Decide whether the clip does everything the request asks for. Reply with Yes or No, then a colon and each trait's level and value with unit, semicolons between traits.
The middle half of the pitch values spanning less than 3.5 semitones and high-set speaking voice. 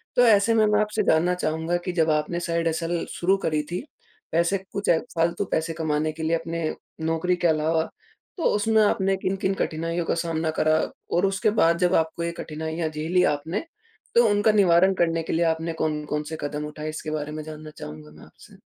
No: narrow, 2.6 semitones; medium, 165 Hz